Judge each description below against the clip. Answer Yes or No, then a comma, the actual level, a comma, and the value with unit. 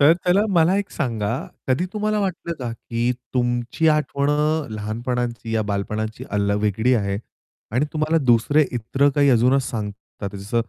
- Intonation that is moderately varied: No, wide, 5.7 semitones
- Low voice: Yes, low, 125 Hz